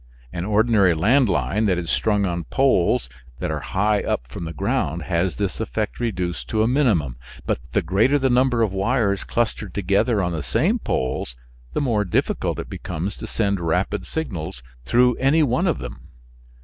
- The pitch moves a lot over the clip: Yes, wide, 5.8 semitones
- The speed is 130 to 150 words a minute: No, average, 180 wpm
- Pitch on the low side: Yes, low, 100 Hz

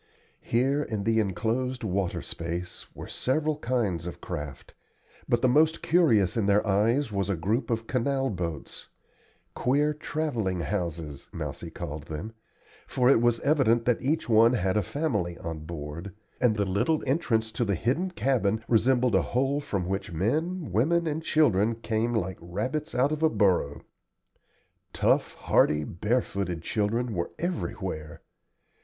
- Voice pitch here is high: No, low, 110 Hz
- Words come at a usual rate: Yes, average, 150 wpm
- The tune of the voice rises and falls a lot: Yes, wide, 6.2 semitones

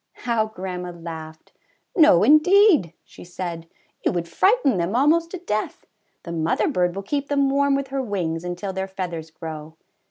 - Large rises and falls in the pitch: Yes, wide, 8.5 semitones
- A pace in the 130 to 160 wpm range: No, average, 170 wpm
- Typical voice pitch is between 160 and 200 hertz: Yes, high, 190 Hz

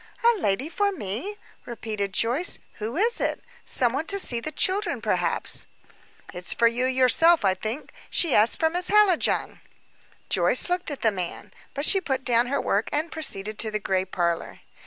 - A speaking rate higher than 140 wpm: Yes, average, 175 wpm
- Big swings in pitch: Yes, wide, 8.2 semitones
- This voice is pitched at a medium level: No, very high, 255 Hz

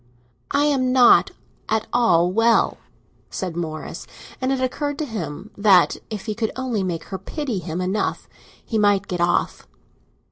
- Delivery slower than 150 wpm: No, average, 155 wpm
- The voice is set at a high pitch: Yes, high, 215 Hz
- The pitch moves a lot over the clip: Yes, wide, 5.7 semitones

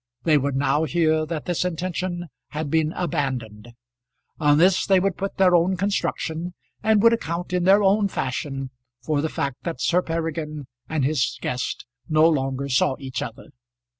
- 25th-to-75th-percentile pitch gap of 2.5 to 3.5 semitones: No, average, 4.3 semitones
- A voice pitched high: No, medium, 160 Hz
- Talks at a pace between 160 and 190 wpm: Yes, average, 165 wpm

